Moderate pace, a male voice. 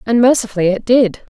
No: average, 180 wpm; female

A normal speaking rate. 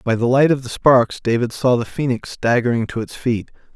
No: fast, 225 wpm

